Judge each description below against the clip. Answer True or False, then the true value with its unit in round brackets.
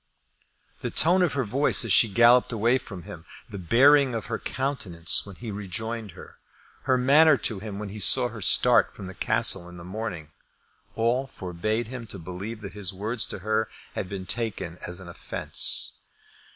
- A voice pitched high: False (110 Hz)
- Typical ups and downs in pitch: True (4.3 semitones)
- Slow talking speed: False (185 wpm)